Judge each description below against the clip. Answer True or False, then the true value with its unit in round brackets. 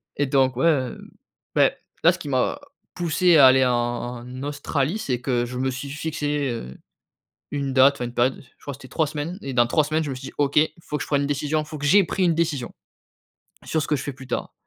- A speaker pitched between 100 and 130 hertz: False (140 Hz)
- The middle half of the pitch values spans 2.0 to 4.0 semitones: True (2.9 semitones)